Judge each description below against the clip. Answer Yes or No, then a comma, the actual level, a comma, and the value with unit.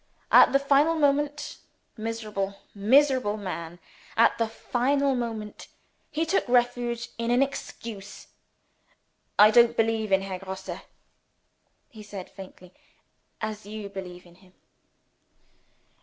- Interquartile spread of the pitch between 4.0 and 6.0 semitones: Yes, average, 4.3 semitones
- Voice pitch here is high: Yes, high, 225 Hz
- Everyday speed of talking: No, slow, 115 wpm